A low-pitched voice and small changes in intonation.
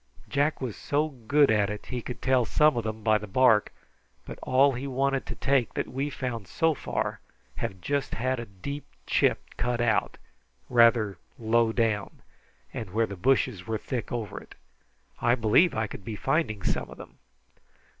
No: low, 120 Hz; average, 3.7 semitones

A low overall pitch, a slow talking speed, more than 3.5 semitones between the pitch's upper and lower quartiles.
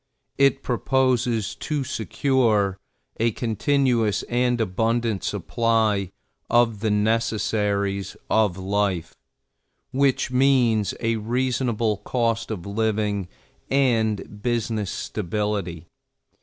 No: low, 110 Hz; slow, 90 wpm; average, 2.8 semitones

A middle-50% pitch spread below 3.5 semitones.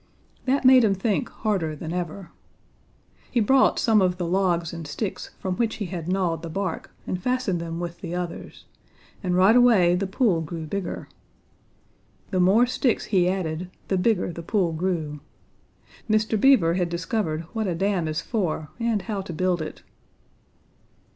No: average, 4.0 semitones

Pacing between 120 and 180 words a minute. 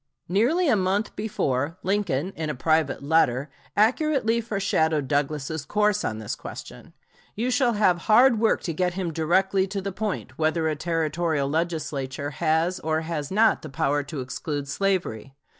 Yes: average, 160 wpm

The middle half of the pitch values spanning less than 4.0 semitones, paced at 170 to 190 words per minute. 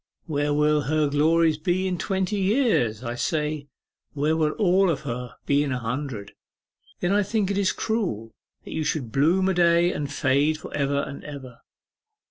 No: average, 4.3 semitones; average, 180 wpm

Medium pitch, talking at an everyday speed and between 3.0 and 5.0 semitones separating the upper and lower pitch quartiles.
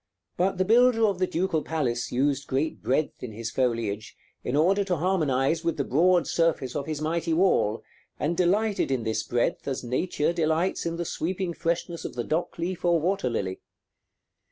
No: medium, 160 Hz; average, 180 wpm; wide, 5.4 semitones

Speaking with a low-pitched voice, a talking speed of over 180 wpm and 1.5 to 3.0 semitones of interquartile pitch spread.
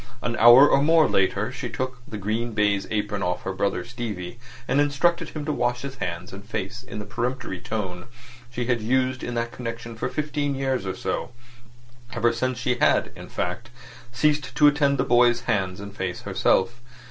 No: low, 120 Hz; average, 190 wpm; average, 3.7 semitones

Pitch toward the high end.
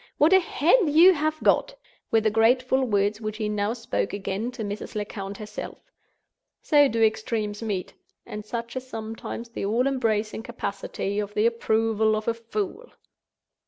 Yes: high, 225 Hz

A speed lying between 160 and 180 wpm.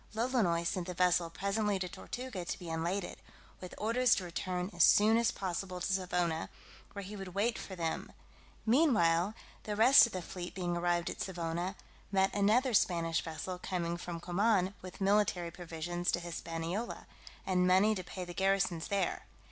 Yes: average, 170 wpm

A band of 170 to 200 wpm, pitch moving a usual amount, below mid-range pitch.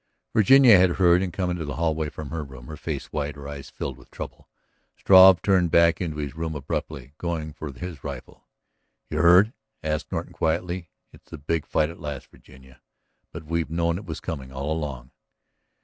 Yes: average, 190 wpm; average, 3.2 semitones; very low, 80 Hz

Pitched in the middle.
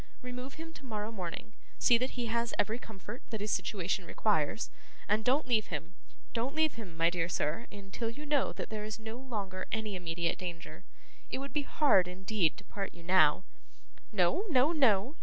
No: high, 215 Hz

